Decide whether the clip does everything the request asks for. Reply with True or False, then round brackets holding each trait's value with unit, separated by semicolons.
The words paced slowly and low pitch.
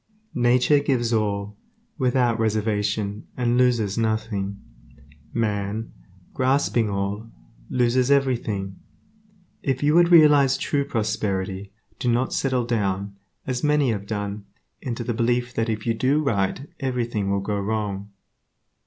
True (125 wpm; 115 Hz)